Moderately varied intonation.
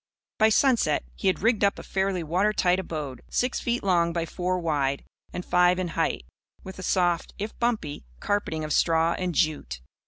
Yes: average, 3.5 semitones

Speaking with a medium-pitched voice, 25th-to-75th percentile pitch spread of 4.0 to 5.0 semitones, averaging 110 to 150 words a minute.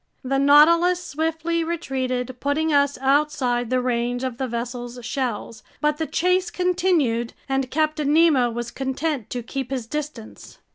No: very high, 275 Hz; average, 4.3 semitones; average, 145 wpm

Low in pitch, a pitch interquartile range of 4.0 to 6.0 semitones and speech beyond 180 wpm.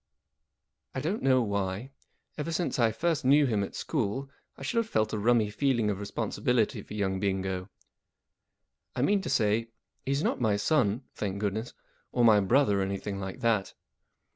No: low, 110 Hz; average, 4.9 semitones; average, 170 wpm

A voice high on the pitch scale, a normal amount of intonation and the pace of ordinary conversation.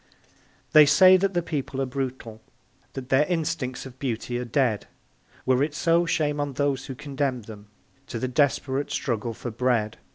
No: low, 135 Hz; average, 3.1 semitones; average, 170 wpm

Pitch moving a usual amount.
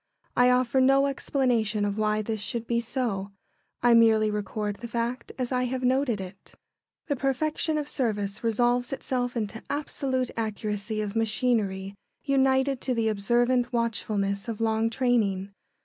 Yes: average, 3.2 semitones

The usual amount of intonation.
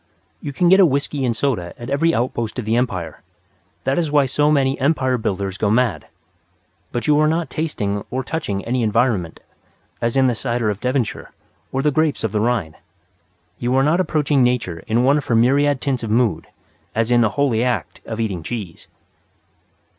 Yes: average, 4.2 semitones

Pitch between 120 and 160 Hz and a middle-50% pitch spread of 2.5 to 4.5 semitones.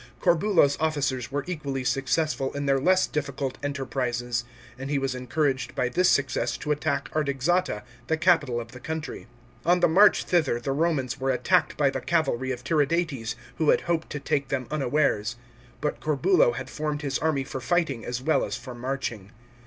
Yes: medium, 140 Hz; average, 3.7 semitones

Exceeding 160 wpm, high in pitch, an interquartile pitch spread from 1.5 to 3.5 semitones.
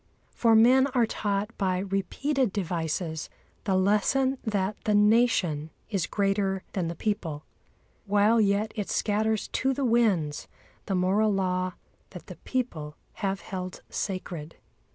No: slow, 135 wpm; high, 200 Hz; average, 3.2 semitones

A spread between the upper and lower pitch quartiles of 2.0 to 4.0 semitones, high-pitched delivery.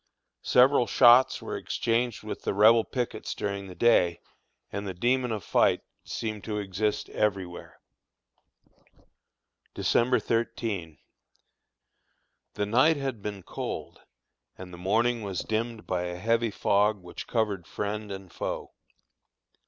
No: average, 3.3 semitones; low, 105 Hz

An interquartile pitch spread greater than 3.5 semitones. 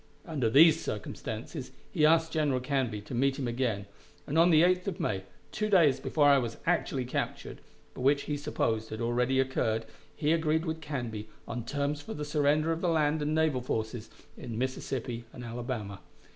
Yes: average, 4.6 semitones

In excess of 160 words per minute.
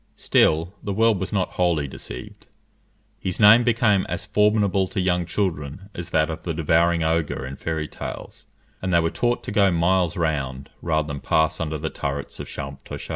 Yes: average, 180 wpm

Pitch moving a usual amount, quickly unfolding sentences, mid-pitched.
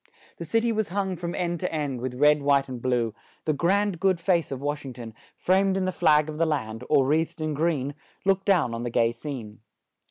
No: wide, 5.7 semitones; fast, 230 wpm; medium, 150 Hz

